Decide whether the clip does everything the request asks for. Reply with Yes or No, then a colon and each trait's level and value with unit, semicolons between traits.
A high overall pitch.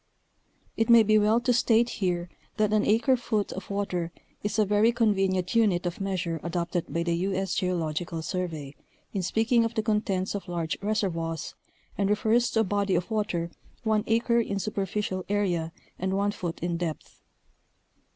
Yes: high, 195 Hz